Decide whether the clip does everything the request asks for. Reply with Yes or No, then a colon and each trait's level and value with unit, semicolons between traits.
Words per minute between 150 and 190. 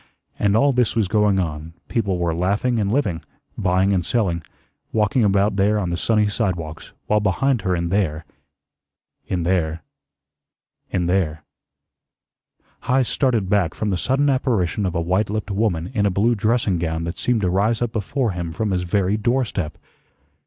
Yes: average, 175 wpm